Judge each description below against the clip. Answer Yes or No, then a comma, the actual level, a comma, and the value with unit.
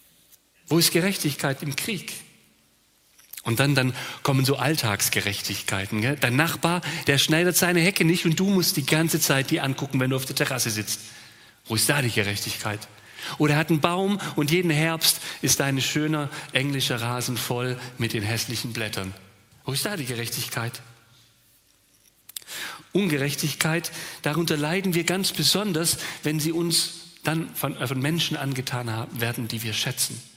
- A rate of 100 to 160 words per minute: Yes, average, 155 wpm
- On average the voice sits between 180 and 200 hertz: No, medium, 140 Hz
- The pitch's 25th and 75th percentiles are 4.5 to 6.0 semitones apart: Yes, wide, 5.5 semitones